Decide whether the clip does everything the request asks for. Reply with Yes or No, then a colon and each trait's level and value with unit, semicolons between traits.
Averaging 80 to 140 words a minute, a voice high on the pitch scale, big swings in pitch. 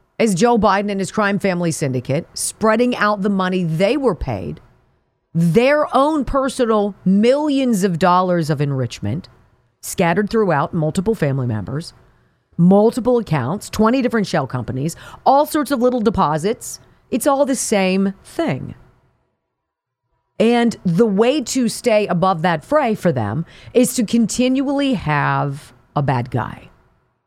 Yes: slow, 135 wpm; high, 200 Hz; wide, 7.5 semitones